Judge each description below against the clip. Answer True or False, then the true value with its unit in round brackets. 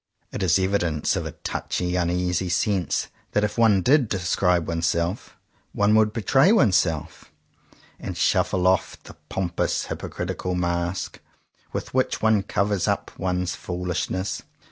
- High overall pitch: False (90 Hz)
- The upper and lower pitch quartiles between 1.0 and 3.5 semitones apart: True (2.8 semitones)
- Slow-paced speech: True (130 wpm)